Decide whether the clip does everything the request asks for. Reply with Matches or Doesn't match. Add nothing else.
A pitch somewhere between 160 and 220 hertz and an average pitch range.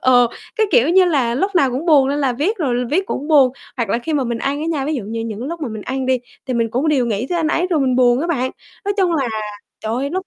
Doesn't match